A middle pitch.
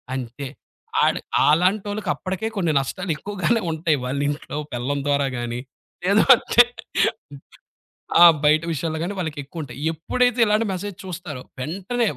Yes: medium, 165 Hz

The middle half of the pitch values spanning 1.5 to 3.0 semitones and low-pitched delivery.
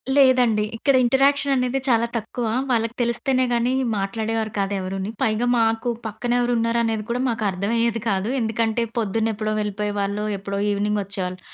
No: narrow, 2.5 semitones; high, 225 Hz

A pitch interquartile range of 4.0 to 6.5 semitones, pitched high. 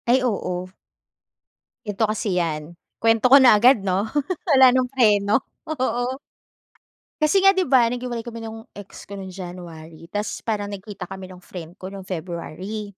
Yes: average, 4.8 semitones; high, 205 Hz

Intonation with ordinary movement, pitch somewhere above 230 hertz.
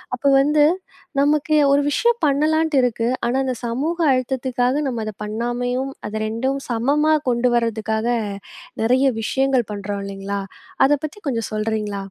Yes: average, 4.0 semitones; high, 245 Hz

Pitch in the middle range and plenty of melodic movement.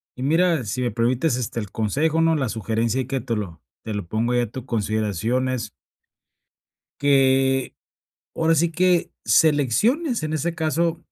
No: low, 130 Hz; wide, 5.9 semitones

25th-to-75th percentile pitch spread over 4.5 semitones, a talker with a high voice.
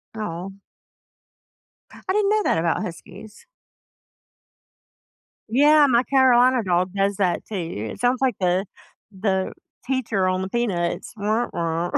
Yes: wide, 5.6 semitones; high, 200 Hz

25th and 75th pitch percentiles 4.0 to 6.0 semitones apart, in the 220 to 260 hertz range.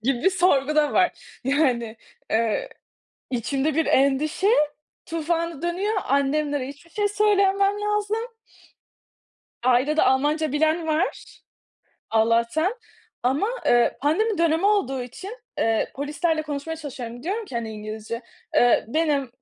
No: wide, 5.4 semitones; very high, 300 Hz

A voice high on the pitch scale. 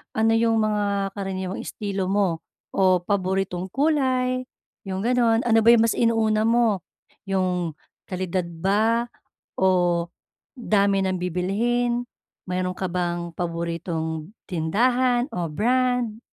Yes: high, 195 Hz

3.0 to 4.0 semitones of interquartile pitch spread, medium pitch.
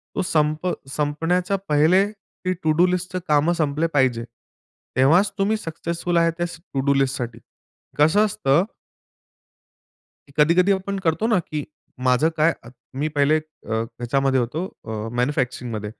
No: average, 4.5 semitones; medium, 155 Hz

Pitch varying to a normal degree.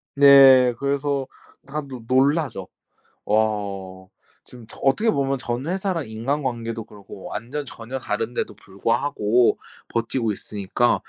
Yes: average, 4.0 semitones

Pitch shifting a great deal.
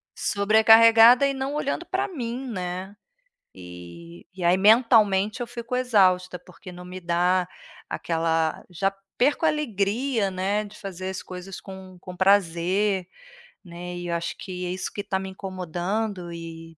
No: average, 3.8 semitones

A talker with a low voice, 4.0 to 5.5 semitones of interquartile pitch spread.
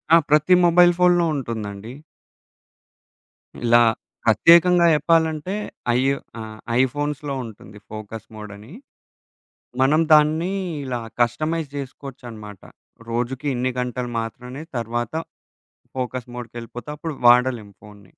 Yes: low, 125 Hz; average, 4.9 semitones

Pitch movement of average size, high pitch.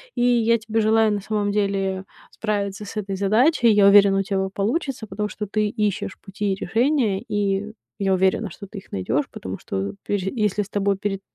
No: narrow, 1.9 semitones; high, 205 Hz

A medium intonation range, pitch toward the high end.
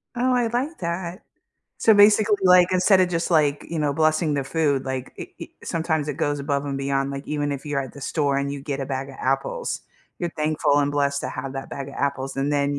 No: average, 3.5 semitones; medium, 145 Hz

